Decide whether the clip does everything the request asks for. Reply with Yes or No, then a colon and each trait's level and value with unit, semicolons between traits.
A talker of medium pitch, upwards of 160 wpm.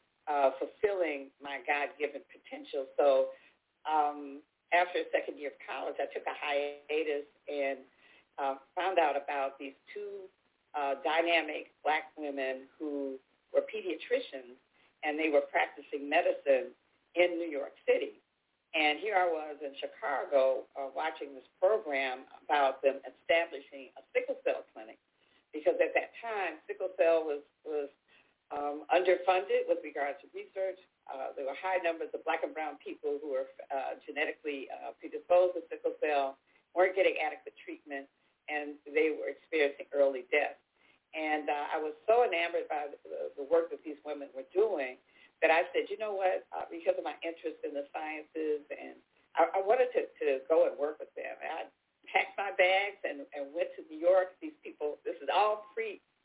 Yes: medium, 175 Hz; average, 170 wpm